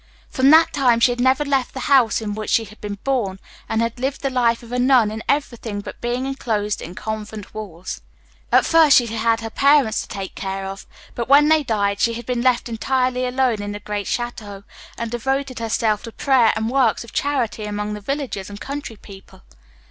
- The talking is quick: Yes, fast, 215 wpm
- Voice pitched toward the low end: No, high, 235 Hz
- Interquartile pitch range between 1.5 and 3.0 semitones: No, average, 3.8 semitones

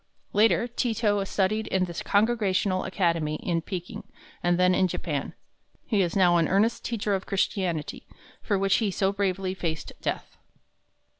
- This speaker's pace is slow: No, average, 155 wpm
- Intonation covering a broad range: No, average, 2.7 semitones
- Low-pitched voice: No, high, 190 Hz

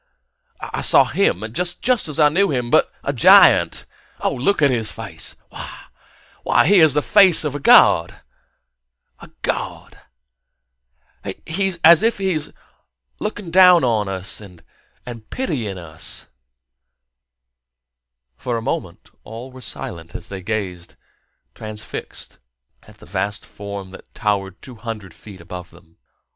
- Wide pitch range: Yes, wide, 8.9 semitones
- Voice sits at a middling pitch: No, low, 115 Hz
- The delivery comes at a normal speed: No, slow, 130 wpm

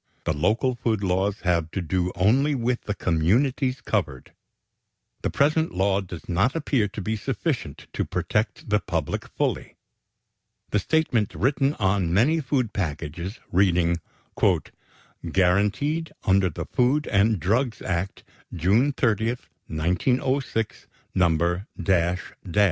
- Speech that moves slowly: Yes, slow, 120 wpm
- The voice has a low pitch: Yes, low, 100 Hz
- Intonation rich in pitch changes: Yes, wide, 6.1 semitones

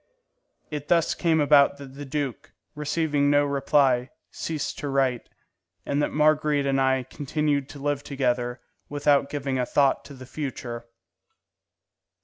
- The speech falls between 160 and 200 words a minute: No, average, 140 wpm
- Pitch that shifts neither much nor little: No, narrow, 1.8 semitones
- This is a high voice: No, medium, 140 Hz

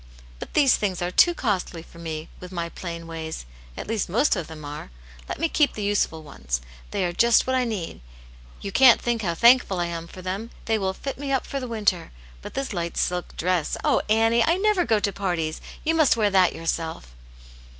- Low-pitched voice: No, high, 190 Hz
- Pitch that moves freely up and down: Yes, wide, 5.7 semitones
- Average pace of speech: No, fast, 220 wpm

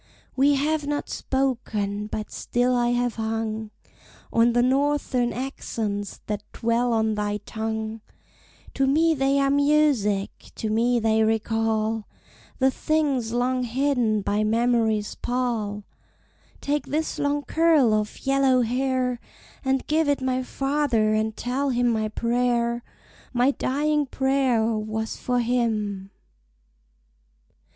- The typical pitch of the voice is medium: No, high, 245 Hz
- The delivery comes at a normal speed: No, slow, 125 wpm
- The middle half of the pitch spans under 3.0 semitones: No, average, 3.6 semitones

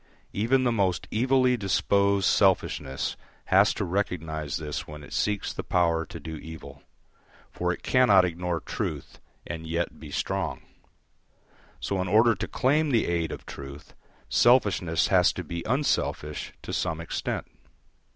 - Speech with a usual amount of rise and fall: Yes, average, 4.8 semitones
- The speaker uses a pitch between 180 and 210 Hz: No, very low, 90 Hz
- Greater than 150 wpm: No, average, 145 wpm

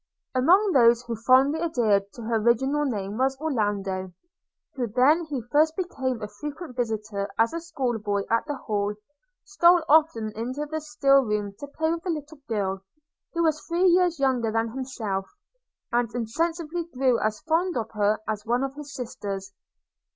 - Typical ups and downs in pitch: No, wide, 6.3 semitones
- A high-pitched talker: Yes, very high, 255 Hz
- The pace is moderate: Yes, average, 170 wpm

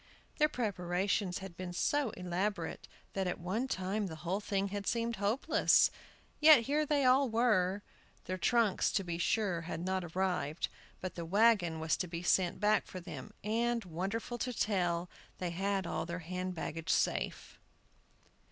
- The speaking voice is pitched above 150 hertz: Yes, high, 190 Hz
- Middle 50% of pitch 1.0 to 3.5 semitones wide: No, average, 4.0 semitones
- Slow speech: No, average, 160 wpm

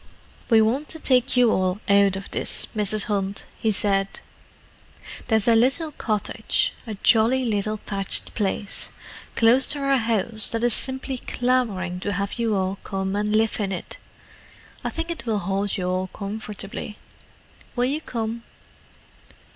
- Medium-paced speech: Yes, average, 145 wpm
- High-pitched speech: Yes, high, 215 Hz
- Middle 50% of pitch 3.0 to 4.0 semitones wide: Yes, average, 3.5 semitones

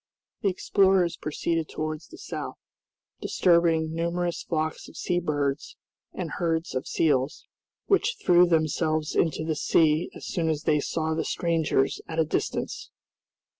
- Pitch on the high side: No, medium, 160 Hz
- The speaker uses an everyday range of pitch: No, narrow, 1.8 semitones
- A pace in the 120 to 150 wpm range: Yes, average, 140 wpm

